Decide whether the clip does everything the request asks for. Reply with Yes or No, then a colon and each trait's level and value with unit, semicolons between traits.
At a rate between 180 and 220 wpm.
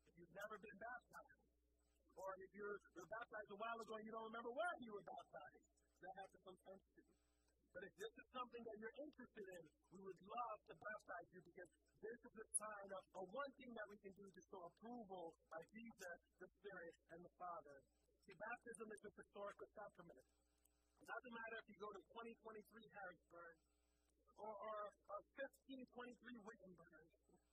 Yes: average, 185 wpm